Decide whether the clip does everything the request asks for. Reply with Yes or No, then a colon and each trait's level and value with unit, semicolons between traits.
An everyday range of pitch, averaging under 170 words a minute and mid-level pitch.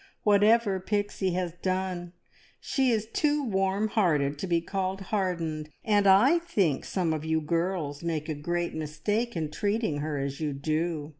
Yes: average, 4.7 semitones; average, 160 wpm; medium, 180 Hz